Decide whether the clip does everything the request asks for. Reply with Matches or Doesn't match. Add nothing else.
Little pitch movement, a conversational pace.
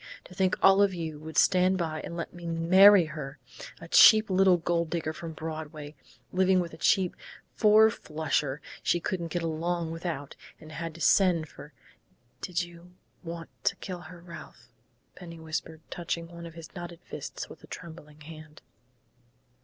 Matches